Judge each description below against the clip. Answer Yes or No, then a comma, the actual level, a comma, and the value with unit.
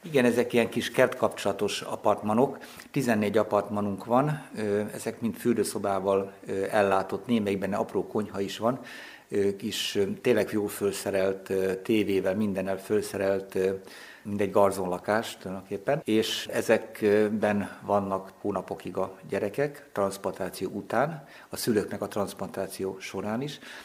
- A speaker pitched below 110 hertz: Yes, low, 100 Hz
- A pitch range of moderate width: No, narrow, 2.2 semitones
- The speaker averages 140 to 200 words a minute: No, average, 110 wpm